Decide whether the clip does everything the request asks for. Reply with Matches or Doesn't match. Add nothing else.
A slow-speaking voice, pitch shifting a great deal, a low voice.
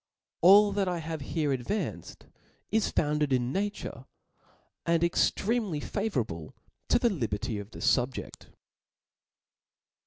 Doesn't match